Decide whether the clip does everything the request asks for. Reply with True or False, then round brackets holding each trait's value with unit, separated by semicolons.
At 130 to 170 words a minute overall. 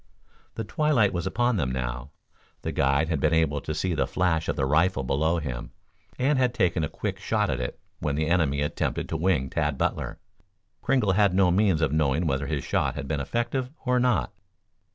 False (200 wpm)